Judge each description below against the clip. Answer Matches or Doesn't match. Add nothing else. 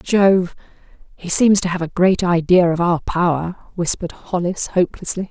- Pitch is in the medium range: Matches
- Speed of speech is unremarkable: Matches